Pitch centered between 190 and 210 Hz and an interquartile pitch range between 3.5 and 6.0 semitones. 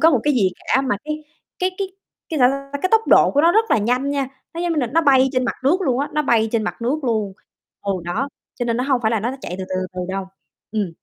No: very high, 260 Hz; average, 5.3 semitones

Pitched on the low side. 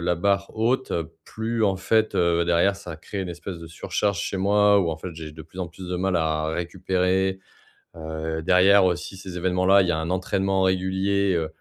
Yes: very low, 90 Hz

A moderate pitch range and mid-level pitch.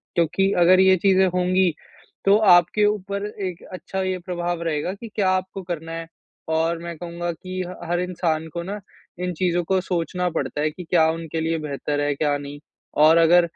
No: narrow, 2.3 semitones; medium, 175 Hz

